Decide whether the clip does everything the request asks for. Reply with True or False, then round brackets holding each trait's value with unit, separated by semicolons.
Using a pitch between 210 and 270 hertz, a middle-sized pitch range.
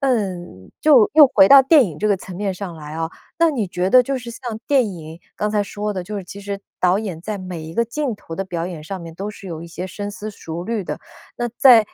False (200 Hz; 4.9 semitones)